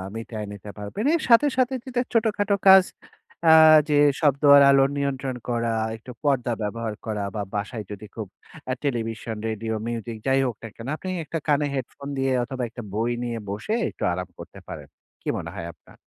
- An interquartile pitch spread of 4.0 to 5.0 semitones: Yes, average, 4.7 semitones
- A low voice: Yes, low, 125 Hz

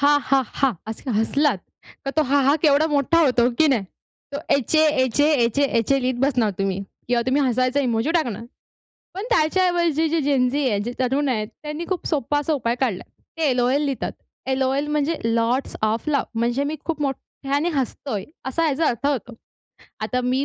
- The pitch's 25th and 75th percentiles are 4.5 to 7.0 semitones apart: No, average, 3.4 semitones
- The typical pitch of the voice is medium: No, very high, 275 Hz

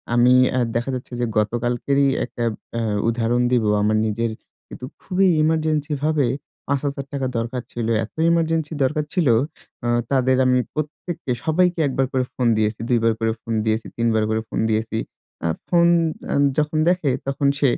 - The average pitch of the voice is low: Yes, low, 130 Hz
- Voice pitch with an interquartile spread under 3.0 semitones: No, average, 4.6 semitones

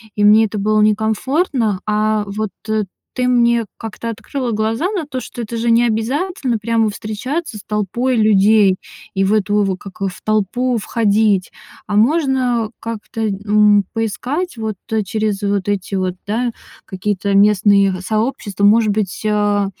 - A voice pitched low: No, high, 215 Hz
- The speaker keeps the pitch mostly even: Yes, narrow, 2.3 semitones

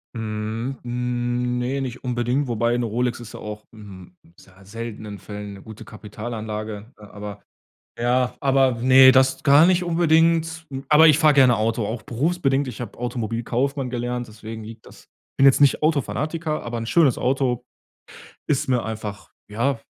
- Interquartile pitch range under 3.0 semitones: No, average, 3.7 semitones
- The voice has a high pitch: No, low, 120 Hz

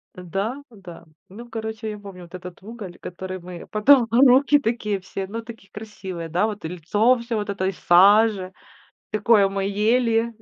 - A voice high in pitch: Yes, high, 210 Hz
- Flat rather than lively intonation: No, average, 3.5 semitones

